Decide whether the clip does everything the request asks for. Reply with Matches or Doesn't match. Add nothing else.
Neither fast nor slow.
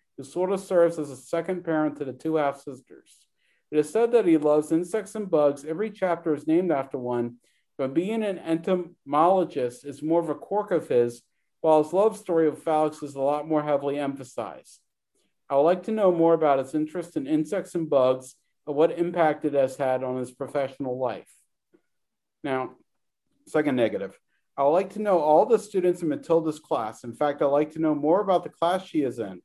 Doesn't match